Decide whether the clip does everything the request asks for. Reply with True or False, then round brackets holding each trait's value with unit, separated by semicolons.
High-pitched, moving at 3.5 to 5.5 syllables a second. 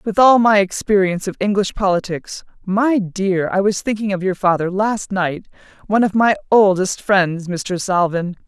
True (195 Hz; 4.6 syllables/s)